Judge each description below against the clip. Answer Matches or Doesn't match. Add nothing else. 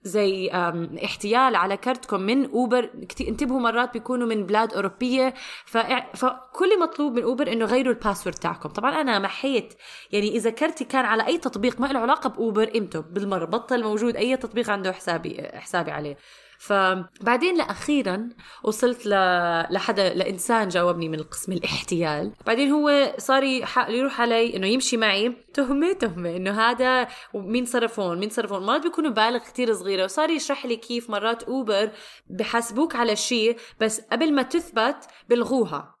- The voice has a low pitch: Doesn't match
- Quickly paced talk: Matches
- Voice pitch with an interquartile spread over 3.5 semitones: Matches